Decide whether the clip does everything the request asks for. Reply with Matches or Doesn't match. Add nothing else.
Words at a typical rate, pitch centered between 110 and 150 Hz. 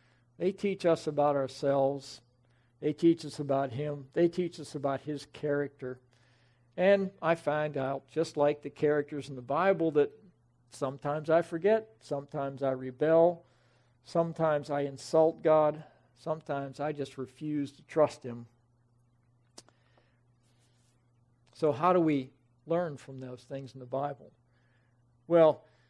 Doesn't match